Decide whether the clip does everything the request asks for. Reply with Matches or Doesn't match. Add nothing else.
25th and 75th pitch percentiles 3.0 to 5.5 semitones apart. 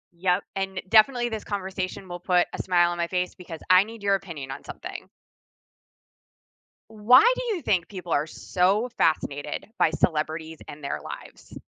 Matches